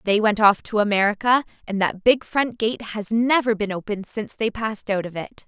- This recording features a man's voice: No, female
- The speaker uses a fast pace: Yes, fast, 220 wpm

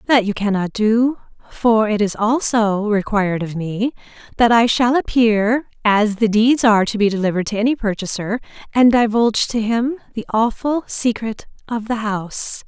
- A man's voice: No, female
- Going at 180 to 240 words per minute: No, average, 165 wpm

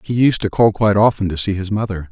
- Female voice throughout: No, male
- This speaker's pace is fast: Yes, fast, 285 wpm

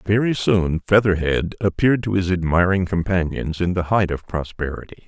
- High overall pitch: No, very low, 90 Hz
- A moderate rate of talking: Yes, average, 155 wpm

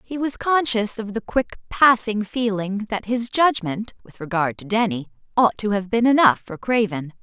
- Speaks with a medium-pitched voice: No, high, 215 Hz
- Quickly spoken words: No, average, 185 wpm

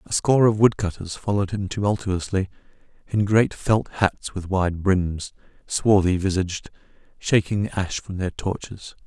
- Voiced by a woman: No, male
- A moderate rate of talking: No, slow, 130 wpm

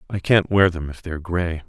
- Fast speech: Yes, fast, 285 wpm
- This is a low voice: Yes, very low, 90 Hz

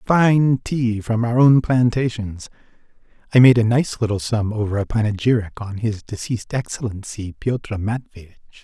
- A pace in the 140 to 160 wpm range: Yes, average, 145 wpm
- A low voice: Yes, low, 115 Hz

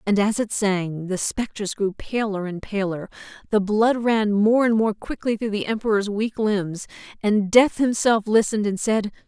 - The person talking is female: Yes, female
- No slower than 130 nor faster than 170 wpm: No, average, 180 wpm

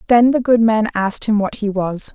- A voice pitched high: Yes, high, 215 Hz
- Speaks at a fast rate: Yes, fast, 250 wpm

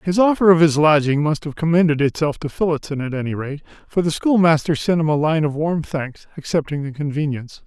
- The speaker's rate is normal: No, fast, 210 wpm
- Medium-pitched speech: Yes, medium, 155 Hz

